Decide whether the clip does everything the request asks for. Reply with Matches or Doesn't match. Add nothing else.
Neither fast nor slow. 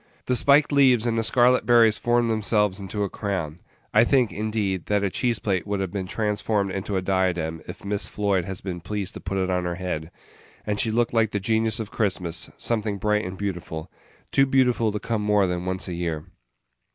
Doesn't match